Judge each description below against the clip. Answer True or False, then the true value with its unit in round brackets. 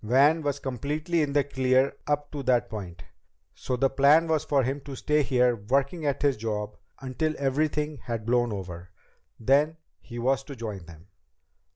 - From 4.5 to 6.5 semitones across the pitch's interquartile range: False (3.9 semitones)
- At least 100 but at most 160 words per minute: False (175 wpm)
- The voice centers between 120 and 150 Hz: True (135 Hz)